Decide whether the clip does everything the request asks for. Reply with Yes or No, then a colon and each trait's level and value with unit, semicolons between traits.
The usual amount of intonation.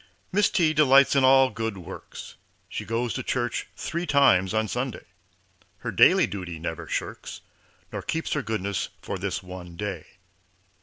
No: wide, 6.4 semitones